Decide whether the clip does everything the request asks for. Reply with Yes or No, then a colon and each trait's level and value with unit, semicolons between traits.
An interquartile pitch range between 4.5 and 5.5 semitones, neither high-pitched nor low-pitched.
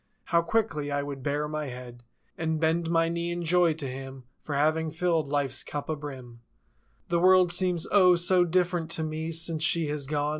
No: average, 3.0 semitones; medium, 160 Hz